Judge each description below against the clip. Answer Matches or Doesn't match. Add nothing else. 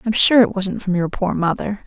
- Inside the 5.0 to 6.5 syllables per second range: Matches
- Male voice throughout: Doesn't match